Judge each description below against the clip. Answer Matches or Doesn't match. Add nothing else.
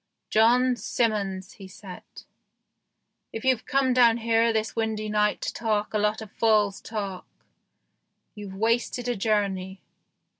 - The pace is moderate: Matches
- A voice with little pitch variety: Matches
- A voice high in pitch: Matches